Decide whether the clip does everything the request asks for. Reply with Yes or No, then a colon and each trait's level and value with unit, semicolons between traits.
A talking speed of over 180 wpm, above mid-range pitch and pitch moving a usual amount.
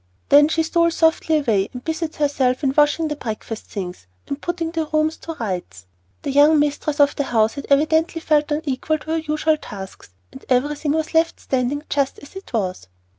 Yes: average, 190 wpm; very high, 295 Hz; average, 3.8 semitones